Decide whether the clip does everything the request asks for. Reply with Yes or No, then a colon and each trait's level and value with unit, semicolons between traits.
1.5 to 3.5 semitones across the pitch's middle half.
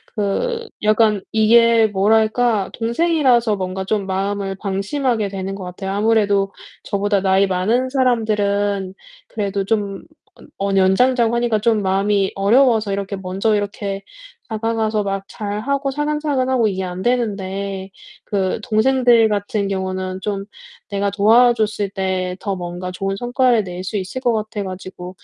Yes: average, 2.9 semitones